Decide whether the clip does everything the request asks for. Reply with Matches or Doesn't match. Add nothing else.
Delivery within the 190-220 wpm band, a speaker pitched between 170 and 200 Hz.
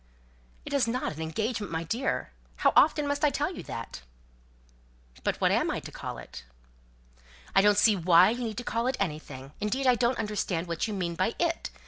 Doesn't match